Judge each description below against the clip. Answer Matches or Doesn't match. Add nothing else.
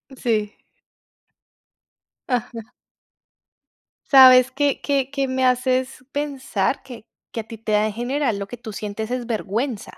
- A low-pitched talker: Doesn't match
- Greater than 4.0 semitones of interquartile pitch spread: Doesn't match